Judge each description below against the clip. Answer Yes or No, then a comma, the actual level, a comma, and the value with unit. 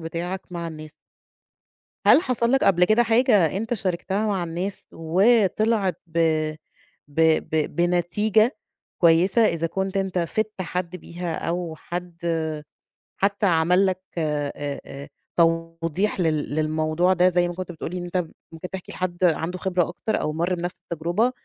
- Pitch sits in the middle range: Yes, medium, 175 Hz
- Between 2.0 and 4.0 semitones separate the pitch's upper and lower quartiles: Yes, narrow, 2.6 semitones